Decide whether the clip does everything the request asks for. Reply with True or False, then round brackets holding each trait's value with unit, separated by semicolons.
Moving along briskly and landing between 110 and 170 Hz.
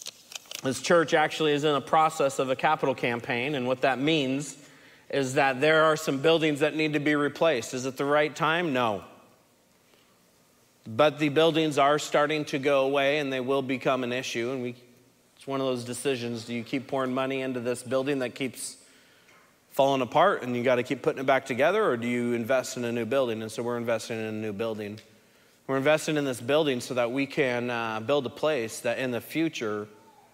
True (210 wpm; 135 Hz)